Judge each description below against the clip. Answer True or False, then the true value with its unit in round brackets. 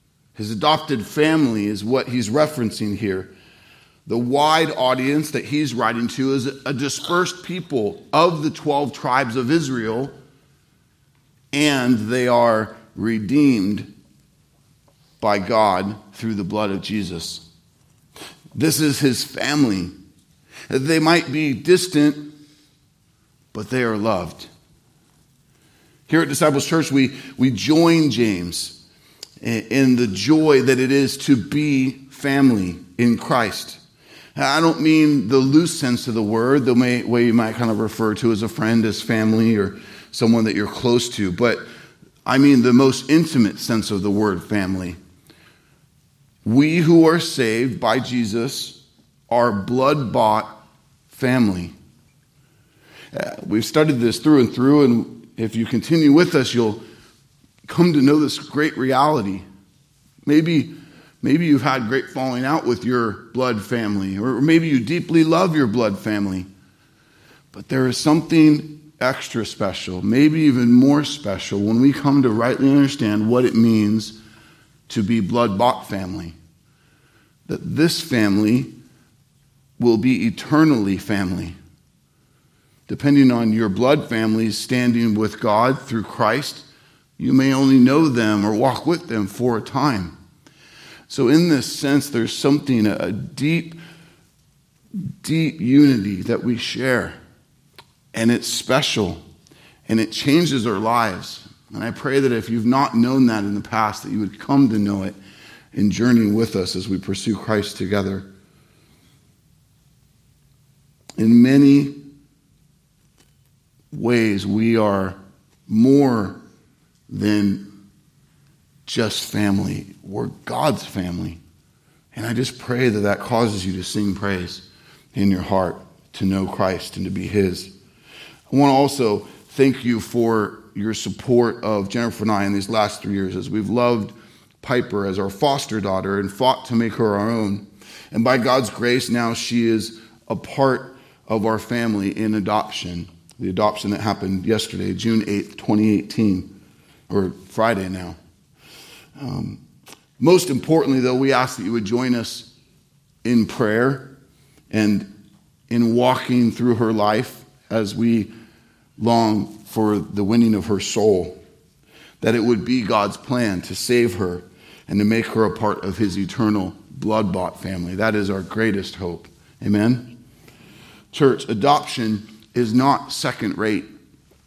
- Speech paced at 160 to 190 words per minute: False (140 wpm)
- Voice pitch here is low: True (120 Hz)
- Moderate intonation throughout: True (4.9 semitones)